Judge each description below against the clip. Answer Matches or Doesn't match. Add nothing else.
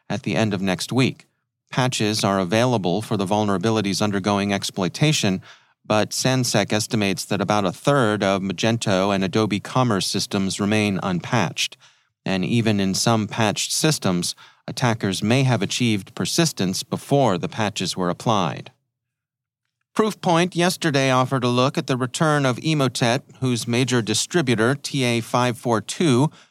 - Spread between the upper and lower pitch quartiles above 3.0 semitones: Matches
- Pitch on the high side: Doesn't match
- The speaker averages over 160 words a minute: Doesn't match